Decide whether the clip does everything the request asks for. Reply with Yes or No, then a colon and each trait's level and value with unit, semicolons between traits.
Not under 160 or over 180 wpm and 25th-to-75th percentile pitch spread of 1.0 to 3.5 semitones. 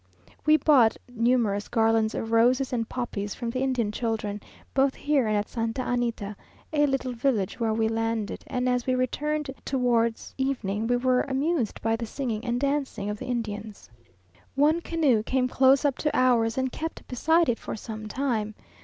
Yes: average, 175 wpm; average, 3.1 semitones